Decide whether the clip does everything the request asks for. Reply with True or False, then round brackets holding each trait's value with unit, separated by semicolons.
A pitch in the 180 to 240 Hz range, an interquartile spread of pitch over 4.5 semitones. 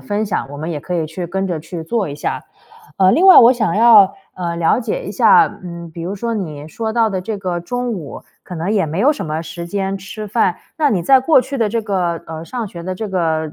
True (190 Hz; 4.9 semitones)